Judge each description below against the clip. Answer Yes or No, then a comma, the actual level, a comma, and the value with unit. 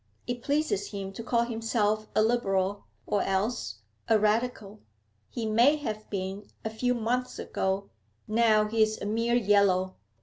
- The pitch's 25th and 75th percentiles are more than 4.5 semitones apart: No, average, 2.7 semitones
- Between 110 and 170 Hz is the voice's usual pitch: No, high, 215 Hz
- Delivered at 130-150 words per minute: Yes, average, 145 wpm